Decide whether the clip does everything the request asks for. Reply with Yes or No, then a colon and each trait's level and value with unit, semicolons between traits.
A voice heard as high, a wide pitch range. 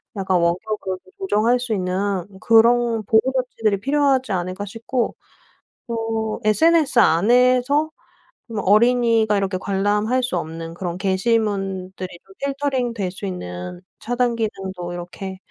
No: high, 215 Hz; average, 4.4 semitones